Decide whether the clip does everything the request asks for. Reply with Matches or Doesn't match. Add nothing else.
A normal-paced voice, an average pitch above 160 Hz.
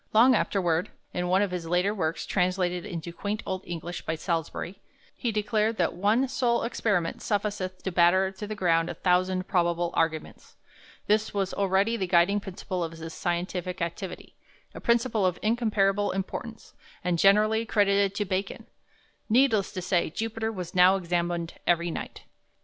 Matches